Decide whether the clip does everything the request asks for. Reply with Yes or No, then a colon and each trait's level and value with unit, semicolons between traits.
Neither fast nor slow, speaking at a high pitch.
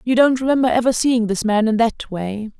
No: fast, 230 wpm; high, 235 Hz